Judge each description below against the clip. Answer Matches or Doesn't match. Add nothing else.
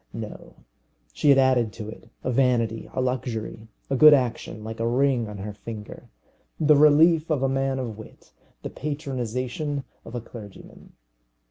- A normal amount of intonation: Matches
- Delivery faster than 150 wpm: Matches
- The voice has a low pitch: Matches